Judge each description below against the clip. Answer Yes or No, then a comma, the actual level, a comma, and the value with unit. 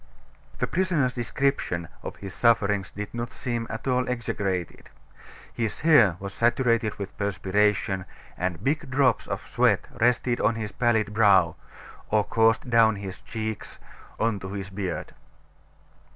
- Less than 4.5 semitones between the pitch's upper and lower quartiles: Yes, average, 3.2 semitones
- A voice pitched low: Yes, low, 110 Hz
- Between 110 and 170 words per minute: Yes, slow, 135 wpm